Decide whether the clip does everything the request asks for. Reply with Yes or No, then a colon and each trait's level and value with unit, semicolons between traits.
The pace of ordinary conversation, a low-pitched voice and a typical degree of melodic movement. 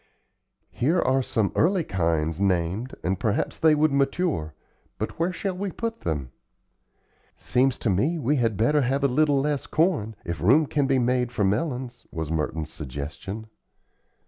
No: average, 160 wpm; low, 125 Hz; wide, 8.5 semitones